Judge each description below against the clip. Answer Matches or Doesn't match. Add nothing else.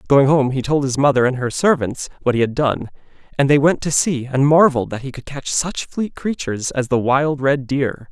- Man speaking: Matches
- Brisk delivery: Matches